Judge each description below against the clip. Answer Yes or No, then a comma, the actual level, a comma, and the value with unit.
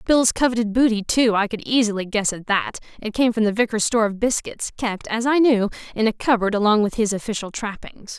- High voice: Yes, high, 220 Hz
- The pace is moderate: No, fast, 220 wpm